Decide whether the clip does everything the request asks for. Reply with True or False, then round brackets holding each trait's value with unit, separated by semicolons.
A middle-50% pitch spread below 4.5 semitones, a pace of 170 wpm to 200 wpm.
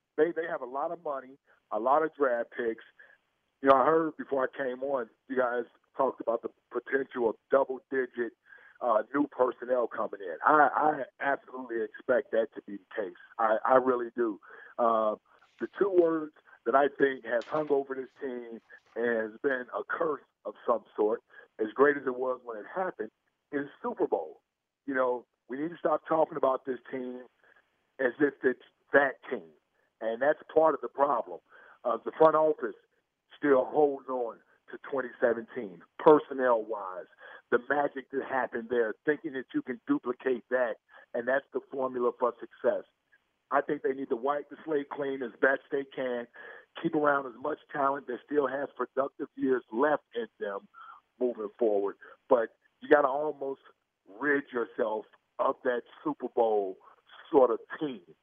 True (3.5 semitones; 175 wpm)